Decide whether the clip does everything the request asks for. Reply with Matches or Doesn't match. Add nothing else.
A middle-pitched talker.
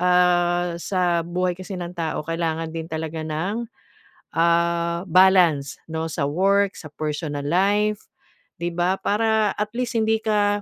Matches